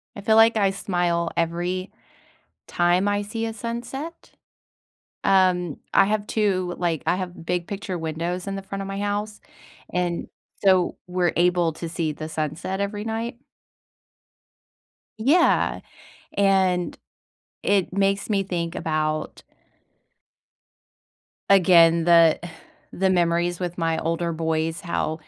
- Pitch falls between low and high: Yes, medium, 180 Hz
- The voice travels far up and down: No, average, 2.9 semitones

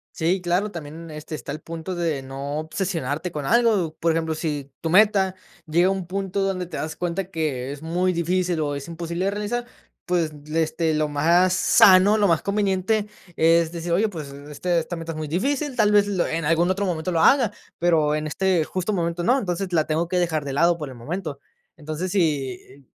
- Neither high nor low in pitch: Yes, medium, 170 Hz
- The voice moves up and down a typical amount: Yes, average, 3.2 semitones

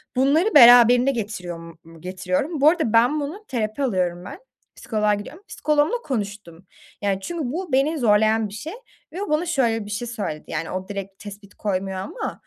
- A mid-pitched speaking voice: No, high, 225 Hz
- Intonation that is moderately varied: No, wide, 6.7 semitones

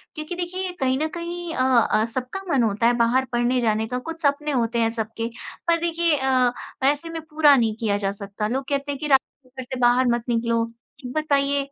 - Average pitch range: Yes, average, 4.6 semitones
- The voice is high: Yes, very high, 260 Hz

